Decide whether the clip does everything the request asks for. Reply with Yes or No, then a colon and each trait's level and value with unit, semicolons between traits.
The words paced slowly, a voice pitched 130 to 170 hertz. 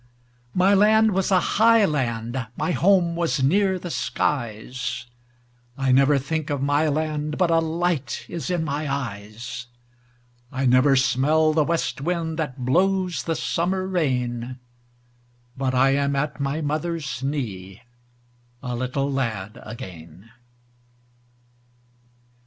Yes: slow, 120 wpm; low, 135 Hz